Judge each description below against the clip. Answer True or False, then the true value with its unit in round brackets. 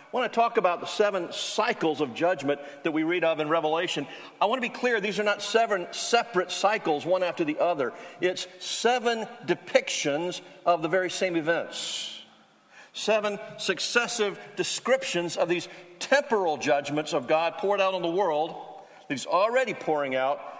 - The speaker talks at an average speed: True (165 wpm)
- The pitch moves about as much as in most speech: True (4.3 semitones)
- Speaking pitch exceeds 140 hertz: True (185 Hz)